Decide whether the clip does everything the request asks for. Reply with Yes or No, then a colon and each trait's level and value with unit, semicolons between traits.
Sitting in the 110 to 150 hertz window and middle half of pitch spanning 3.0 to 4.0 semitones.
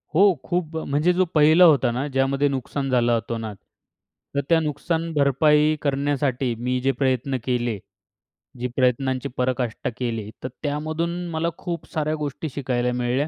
Yes: medium, 140 Hz; average, 3.5 semitones